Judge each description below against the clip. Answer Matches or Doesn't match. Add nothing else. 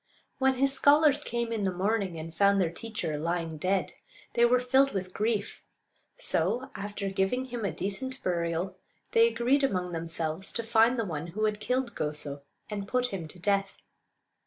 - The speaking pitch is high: Matches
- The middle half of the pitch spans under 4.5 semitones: Doesn't match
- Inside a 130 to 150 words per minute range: Doesn't match